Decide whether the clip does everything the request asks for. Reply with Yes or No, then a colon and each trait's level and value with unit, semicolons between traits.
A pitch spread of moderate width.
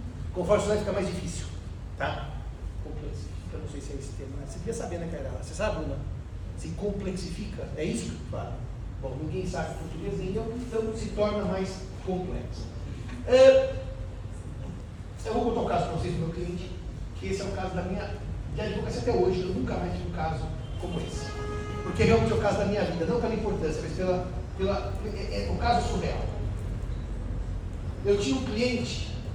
No: wide, 7.1 semitones